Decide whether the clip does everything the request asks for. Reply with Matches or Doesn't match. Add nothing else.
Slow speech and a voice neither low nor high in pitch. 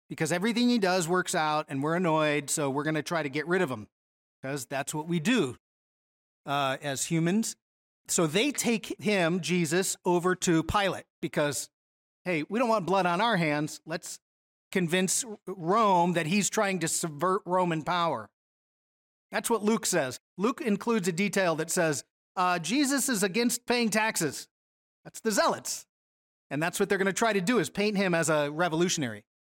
Doesn't match